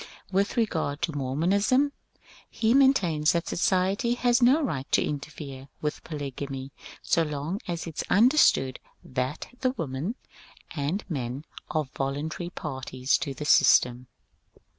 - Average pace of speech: No, slow, 130 wpm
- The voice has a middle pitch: Yes, medium, 155 Hz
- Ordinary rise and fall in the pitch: No, wide, 6.4 semitones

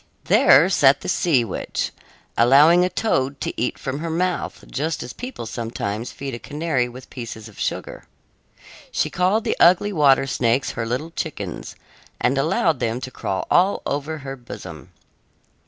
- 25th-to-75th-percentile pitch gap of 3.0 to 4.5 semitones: No, average, 5.3 semitones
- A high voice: No, low, 135 Hz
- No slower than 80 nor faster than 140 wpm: No, average, 160 wpm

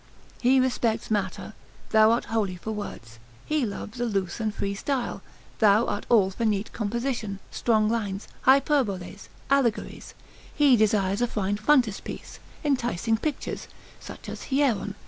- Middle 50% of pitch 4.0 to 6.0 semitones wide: No, average, 3.3 semitones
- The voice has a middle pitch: No, high, 220 Hz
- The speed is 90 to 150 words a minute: Yes, average, 140 wpm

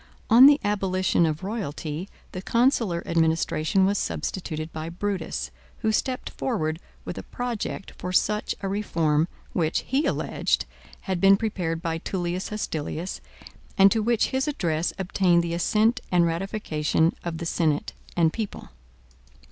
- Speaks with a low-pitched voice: No, medium, 185 Hz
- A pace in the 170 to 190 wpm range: No, average, 140 wpm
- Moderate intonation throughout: Yes, average, 4.4 semitones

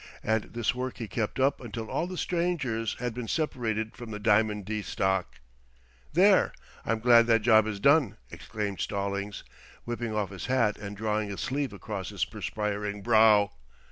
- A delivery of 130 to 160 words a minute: No, average, 170 wpm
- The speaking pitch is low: Yes, low, 110 Hz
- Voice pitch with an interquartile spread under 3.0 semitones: Yes, narrow, 2.5 semitones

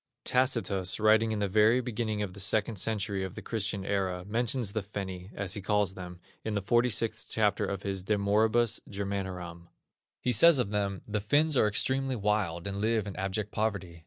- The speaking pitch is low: Yes, low, 105 Hz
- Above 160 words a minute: Yes, average, 190 wpm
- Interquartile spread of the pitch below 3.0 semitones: Yes, narrow, 2.4 semitones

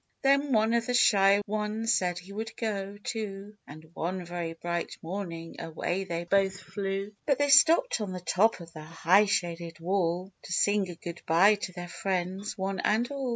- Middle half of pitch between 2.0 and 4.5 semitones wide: Yes, average, 3.5 semitones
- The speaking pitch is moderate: No, high, 195 Hz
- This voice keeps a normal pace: Yes, average, 190 wpm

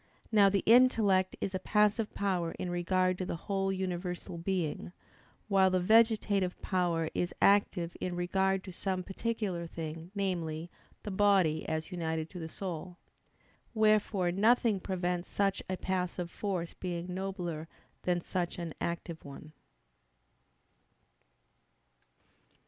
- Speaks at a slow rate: Yes, slow, 125 wpm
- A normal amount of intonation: No, narrow, 2.3 semitones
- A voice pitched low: No, medium, 185 Hz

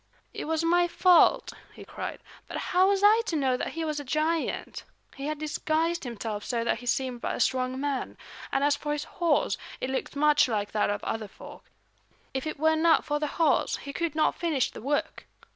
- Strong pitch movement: No, average, 3.8 semitones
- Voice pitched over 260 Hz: Yes, very high, 295 Hz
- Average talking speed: No, fast, 210 wpm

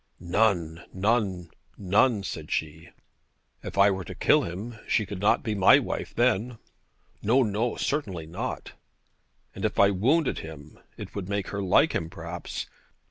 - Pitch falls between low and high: No, low, 100 Hz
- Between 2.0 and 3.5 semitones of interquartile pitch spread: No, average, 4.1 semitones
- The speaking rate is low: No, average, 155 wpm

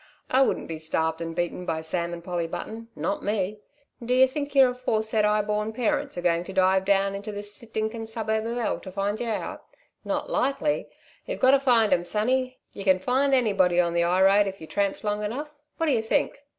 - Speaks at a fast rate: Yes, fast, 210 wpm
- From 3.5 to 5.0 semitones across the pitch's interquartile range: Yes, average, 4.5 semitones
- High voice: Yes, high, 210 Hz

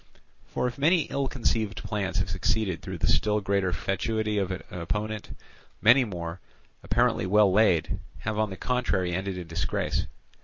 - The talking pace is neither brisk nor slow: Yes, average, 160 wpm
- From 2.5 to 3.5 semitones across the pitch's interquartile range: Yes, average, 3.0 semitones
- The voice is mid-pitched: No, low, 100 Hz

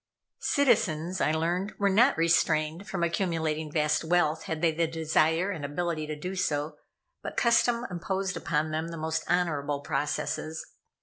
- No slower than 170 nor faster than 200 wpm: No, average, 150 wpm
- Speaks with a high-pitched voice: No, medium, 165 Hz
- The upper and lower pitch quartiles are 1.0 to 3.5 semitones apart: Yes, average, 2.8 semitones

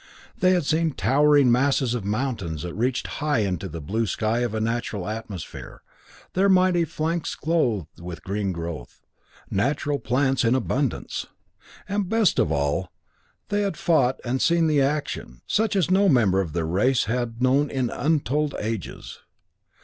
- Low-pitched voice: Yes, low, 125 Hz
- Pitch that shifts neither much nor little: No, wide, 7.1 semitones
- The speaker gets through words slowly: No, average, 155 wpm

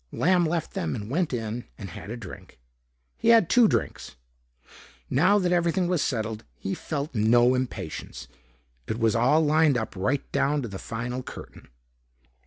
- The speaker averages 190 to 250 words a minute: No, average, 165 wpm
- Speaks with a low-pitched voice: Yes, low, 130 Hz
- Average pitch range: No, wide, 6.9 semitones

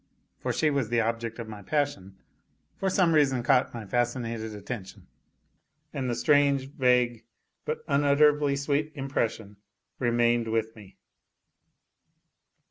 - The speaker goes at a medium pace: No, slow, 125 wpm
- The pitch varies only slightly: No, average, 3.7 semitones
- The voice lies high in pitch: No, low, 125 Hz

